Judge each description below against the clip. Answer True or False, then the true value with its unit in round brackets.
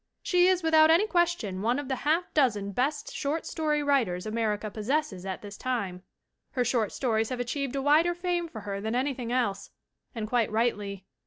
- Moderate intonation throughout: False (6.0 semitones)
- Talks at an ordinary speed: True (185 wpm)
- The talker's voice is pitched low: False (250 Hz)